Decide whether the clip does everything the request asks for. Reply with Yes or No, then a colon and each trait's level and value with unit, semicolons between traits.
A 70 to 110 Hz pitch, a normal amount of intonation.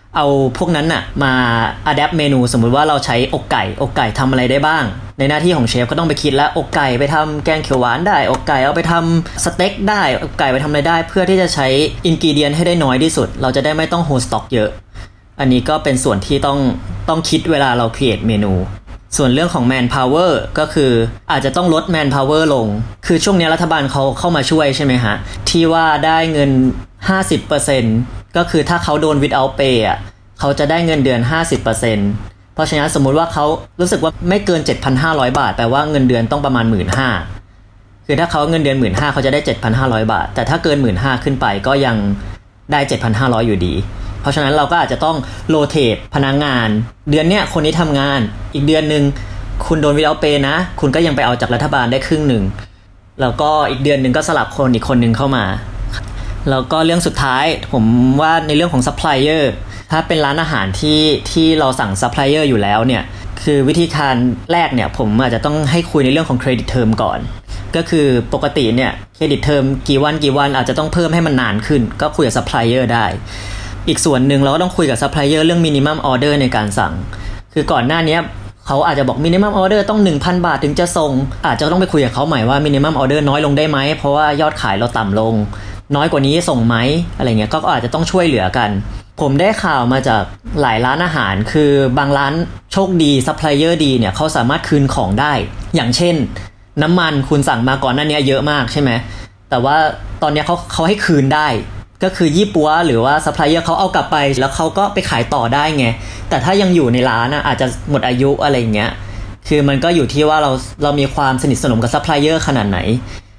No: medium, 140 Hz; average, 4.9 semitones